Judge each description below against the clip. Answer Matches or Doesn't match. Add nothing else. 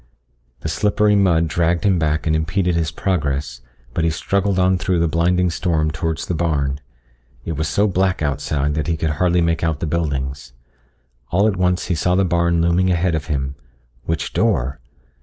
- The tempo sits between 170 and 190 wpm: Matches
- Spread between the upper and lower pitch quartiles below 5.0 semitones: Matches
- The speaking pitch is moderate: Doesn't match